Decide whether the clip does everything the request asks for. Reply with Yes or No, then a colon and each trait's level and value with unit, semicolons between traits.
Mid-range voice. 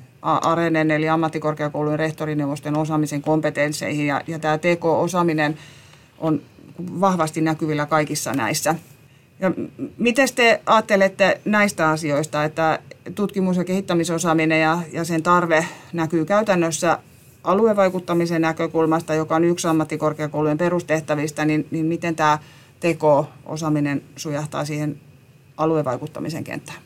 Yes: medium, 155 Hz